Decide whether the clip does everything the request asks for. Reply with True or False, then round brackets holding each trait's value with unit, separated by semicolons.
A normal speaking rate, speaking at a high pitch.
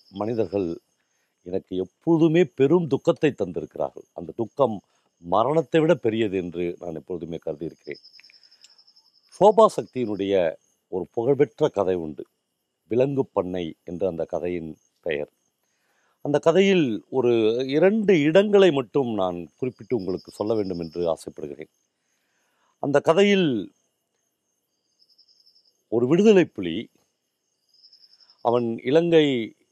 False (95 wpm; 120 Hz)